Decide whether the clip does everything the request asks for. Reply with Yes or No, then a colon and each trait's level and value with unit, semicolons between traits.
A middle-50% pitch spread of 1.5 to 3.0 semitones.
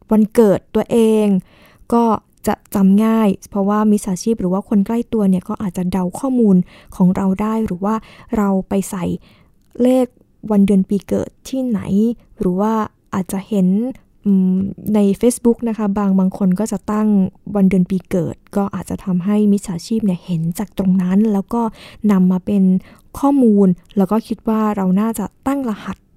Yes: narrow, 2.4 semitones